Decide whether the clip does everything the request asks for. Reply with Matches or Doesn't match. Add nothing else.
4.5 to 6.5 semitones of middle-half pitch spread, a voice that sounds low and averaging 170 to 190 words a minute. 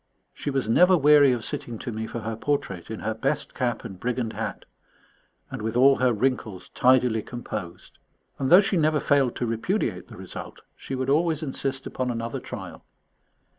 Doesn't match